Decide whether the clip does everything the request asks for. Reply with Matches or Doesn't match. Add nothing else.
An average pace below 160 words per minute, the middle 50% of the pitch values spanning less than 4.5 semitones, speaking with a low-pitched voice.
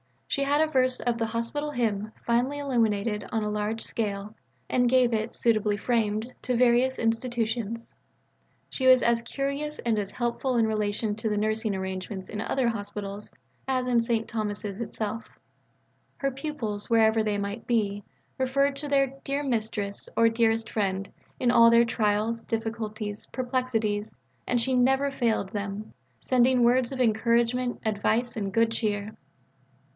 Doesn't match